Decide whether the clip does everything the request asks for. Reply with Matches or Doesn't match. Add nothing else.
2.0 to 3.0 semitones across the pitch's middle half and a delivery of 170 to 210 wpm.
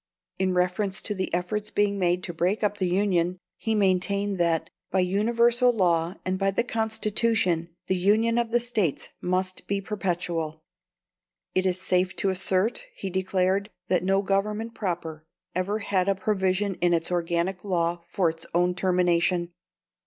Doesn't match